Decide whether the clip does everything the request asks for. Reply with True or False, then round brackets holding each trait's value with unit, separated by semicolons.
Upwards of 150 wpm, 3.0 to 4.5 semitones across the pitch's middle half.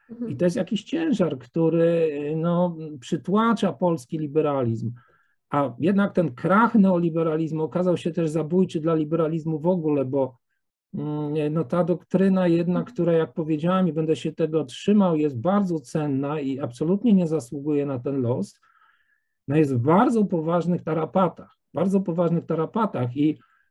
False (140 wpm; 3.3 semitones)